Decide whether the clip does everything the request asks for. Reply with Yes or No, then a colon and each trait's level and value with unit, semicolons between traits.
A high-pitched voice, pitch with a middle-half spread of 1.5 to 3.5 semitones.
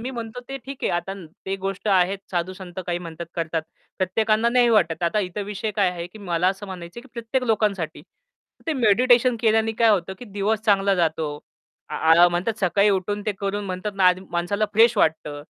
No: high, 195 Hz; average, 4.0 semitones